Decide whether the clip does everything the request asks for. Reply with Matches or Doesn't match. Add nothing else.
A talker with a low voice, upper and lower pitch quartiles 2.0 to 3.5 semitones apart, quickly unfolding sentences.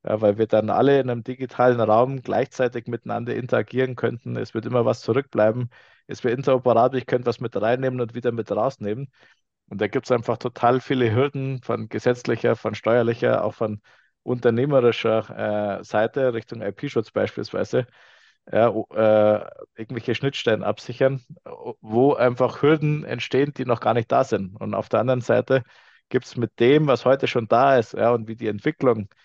Doesn't match